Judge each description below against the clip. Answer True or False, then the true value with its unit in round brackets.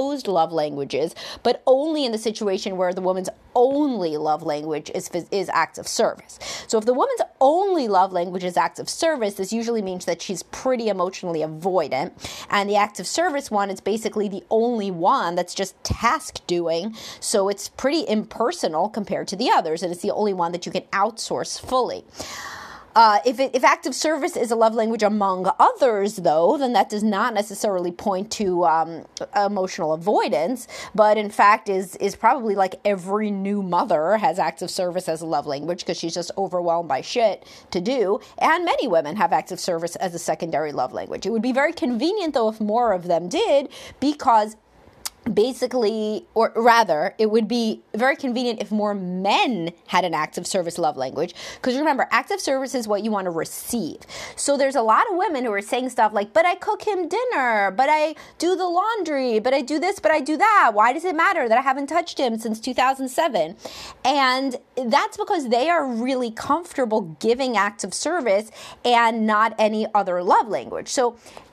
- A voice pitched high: True (220 Hz)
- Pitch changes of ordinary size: False (5.9 semitones)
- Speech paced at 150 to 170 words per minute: False (190 wpm)